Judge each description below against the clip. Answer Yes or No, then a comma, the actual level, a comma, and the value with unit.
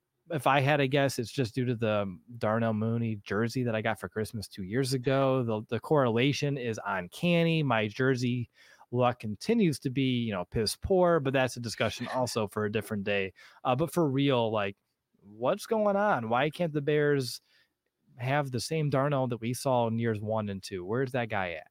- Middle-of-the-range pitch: No, low, 125 Hz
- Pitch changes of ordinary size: Yes, average, 4.1 semitones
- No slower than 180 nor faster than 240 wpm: Yes, average, 200 wpm